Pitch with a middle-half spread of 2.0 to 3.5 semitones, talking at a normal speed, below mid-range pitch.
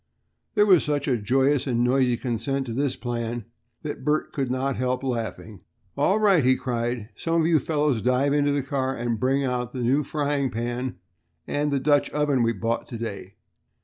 Yes: average, 3.2 semitones; average, 190 wpm; low, 130 Hz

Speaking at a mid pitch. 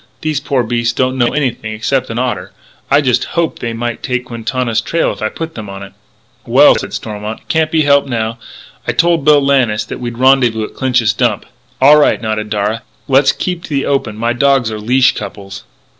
No: low, 125 Hz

